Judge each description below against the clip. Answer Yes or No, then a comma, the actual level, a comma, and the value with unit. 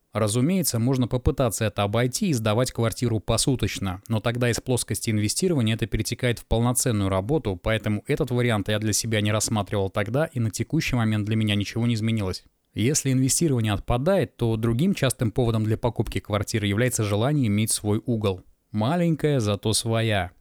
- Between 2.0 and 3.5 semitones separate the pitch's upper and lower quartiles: Yes, average, 2.9 semitones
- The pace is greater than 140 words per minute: Yes, fast, 160 wpm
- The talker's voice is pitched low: Yes, low, 115 Hz